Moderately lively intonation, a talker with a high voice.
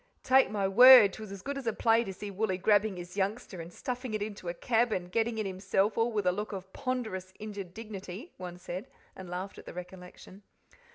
Yes: average, 3.3 semitones; high, 200 Hz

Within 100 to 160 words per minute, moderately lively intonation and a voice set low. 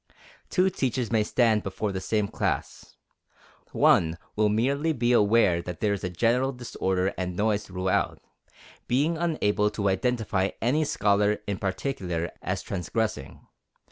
Yes: average, 140 wpm; average, 4.5 semitones; low, 105 Hz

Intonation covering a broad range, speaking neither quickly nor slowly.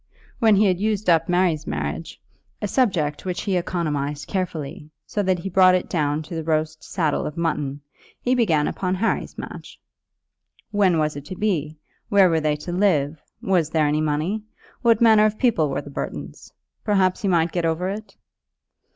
No: average, 4.3 semitones; average, 180 wpm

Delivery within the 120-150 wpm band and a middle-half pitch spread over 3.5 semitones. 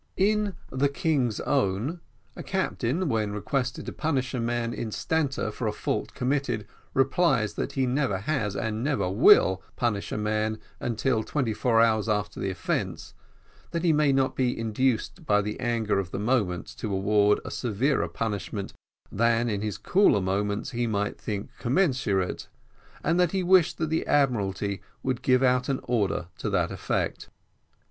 No: average, 165 wpm; average, 4.7 semitones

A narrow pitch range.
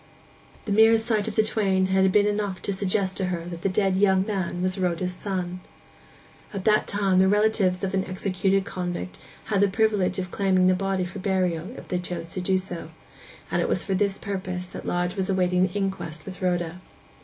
Yes: narrow, 1.6 semitones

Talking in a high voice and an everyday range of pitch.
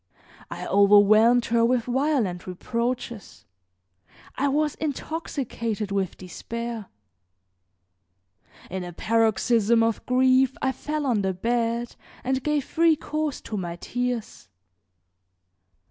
Yes: high, 235 Hz; average, 4.2 semitones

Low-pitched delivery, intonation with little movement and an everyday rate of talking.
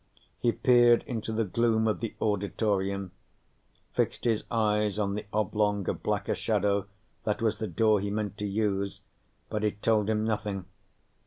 Yes: low, 105 Hz; narrow, 1.6 semitones; average, 160 wpm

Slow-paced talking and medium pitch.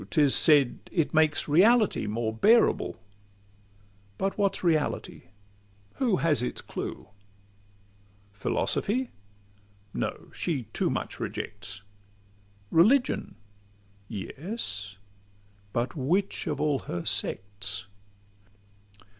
Yes: slow, 90 wpm; medium, 150 Hz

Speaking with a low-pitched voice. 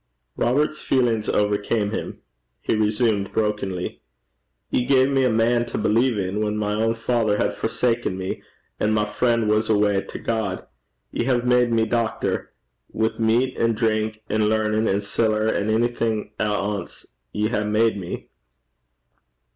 Yes: low, 110 Hz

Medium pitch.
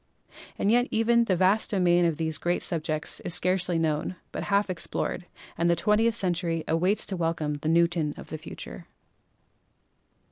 Yes: medium, 175 Hz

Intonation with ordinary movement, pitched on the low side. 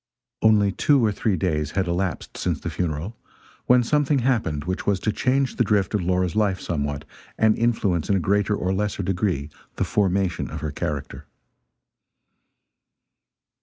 Yes: average, 3.8 semitones; very low, 95 Hz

